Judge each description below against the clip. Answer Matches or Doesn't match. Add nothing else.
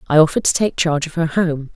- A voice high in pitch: Doesn't match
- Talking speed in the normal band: Doesn't match